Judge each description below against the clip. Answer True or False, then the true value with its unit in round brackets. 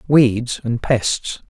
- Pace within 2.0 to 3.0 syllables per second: True (2.4 syllables/s)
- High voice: False (120 Hz)